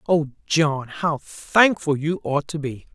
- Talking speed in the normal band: Yes, average, 165 wpm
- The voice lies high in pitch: No, medium, 155 Hz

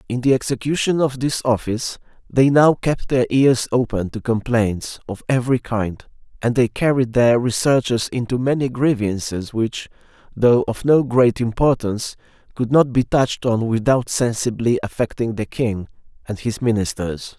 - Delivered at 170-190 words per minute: No, average, 150 wpm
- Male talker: Yes, male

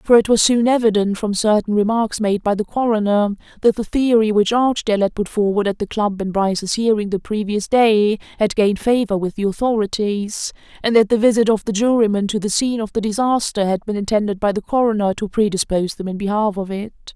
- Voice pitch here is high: Yes, high, 210 Hz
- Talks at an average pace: No, fast, 215 wpm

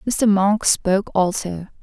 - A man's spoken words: No, female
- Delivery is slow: Yes, slow, 130 wpm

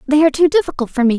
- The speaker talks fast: Yes, fast, 305 wpm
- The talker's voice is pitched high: Yes, very high, 285 Hz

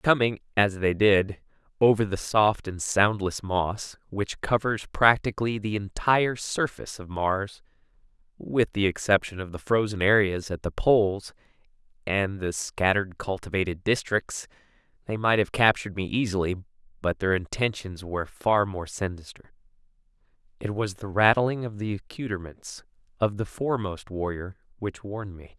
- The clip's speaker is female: No, male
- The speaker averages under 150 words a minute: Yes, average, 140 wpm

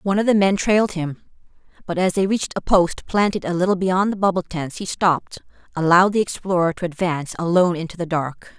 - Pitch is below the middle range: No, medium, 180 Hz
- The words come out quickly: Yes, fast, 210 wpm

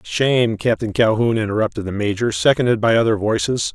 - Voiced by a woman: No, male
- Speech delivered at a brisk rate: No, average, 160 wpm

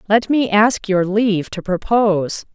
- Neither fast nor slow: Yes, average, 165 wpm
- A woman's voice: Yes, female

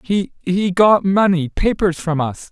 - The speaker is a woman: No, male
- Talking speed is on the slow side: Yes, slow, 95 wpm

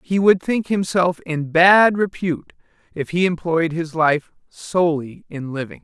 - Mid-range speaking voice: Yes, medium, 170 Hz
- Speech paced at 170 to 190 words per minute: No, average, 155 wpm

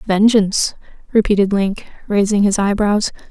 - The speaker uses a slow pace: Yes, slow, 110 wpm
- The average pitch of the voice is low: No, high, 205 Hz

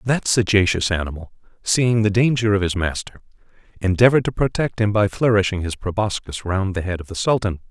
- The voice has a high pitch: No, low, 105 Hz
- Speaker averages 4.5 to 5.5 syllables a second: No, 5.7 syllables/s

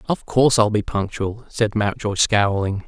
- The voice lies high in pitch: No, low, 110 Hz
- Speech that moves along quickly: No, average, 165 wpm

